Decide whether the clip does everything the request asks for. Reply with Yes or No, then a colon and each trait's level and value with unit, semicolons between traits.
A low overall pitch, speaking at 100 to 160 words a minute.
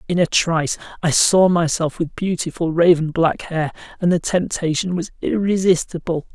No: medium, 170 Hz; average, 150 wpm